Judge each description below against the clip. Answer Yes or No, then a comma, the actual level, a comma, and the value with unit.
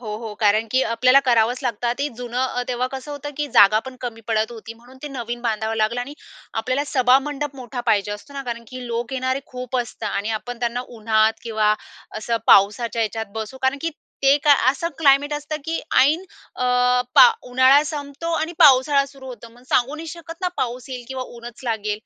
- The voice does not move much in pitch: No, average, 3.5 semitones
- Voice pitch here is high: Yes, very high, 250 Hz